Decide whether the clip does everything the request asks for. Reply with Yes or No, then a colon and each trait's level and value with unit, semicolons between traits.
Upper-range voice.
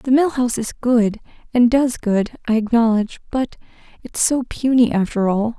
Yes: high, 235 Hz